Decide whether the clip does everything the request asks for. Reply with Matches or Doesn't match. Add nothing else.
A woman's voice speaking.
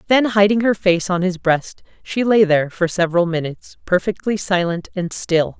Matches